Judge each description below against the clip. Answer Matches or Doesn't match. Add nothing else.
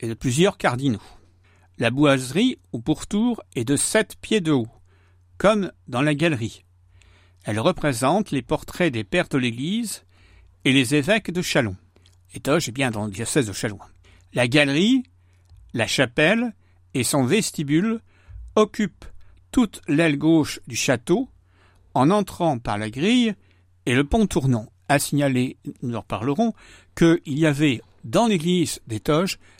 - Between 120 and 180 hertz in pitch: Matches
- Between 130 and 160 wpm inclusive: Matches